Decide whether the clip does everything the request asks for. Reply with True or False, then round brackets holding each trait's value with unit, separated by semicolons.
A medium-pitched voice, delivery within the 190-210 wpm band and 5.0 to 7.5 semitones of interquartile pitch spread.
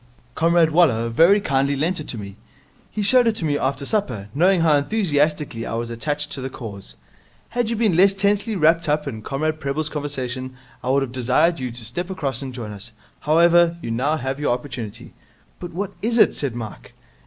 True (145 Hz; 200 wpm; 5.4 semitones)